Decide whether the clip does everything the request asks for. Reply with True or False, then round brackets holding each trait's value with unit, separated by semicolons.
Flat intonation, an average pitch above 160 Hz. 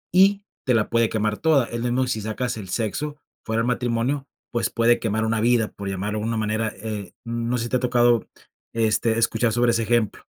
False (1.9 semitones; 115 Hz)